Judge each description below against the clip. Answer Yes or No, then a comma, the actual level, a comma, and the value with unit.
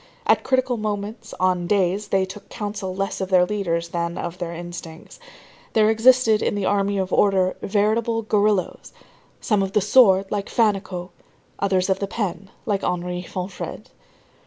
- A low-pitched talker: No, high, 195 Hz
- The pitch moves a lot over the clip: No, narrow, 2.5 semitones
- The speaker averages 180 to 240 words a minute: No, average, 160 wpm